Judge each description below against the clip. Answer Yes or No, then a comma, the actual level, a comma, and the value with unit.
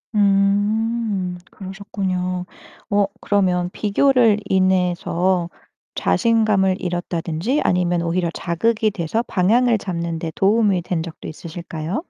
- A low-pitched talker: No, high, 190 Hz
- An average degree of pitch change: Yes, average, 3.1 semitones